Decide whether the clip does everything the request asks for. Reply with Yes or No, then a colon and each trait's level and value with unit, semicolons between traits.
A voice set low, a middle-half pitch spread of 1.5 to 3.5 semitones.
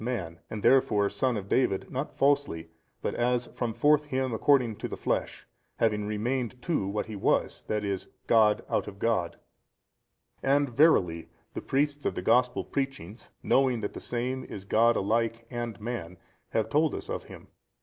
No: low, 120 Hz; average, 4.1 semitones